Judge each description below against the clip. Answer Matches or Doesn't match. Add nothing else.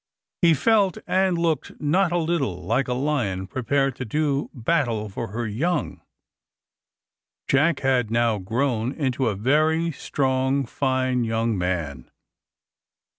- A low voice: Matches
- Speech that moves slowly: Matches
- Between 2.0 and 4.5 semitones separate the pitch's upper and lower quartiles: Doesn't match